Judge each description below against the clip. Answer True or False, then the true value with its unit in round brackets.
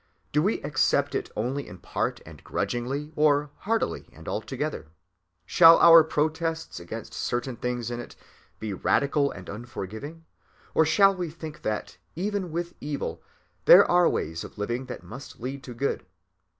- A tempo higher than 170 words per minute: False (155 wpm)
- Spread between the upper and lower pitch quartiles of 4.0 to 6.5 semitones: True (5.5 semitones)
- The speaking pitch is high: False (140 Hz)